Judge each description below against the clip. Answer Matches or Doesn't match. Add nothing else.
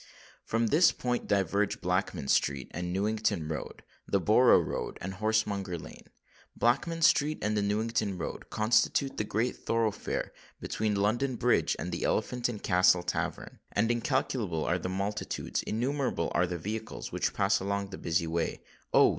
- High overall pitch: Doesn't match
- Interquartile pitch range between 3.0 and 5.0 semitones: Matches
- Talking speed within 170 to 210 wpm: Doesn't match